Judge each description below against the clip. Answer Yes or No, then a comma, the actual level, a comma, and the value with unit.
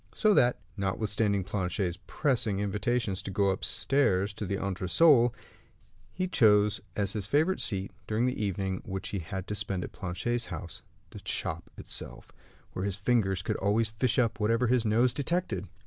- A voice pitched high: No, low, 105 Hz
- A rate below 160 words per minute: No, average, 165 wpm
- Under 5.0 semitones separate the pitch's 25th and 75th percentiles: Yes, average, 3.8 semitones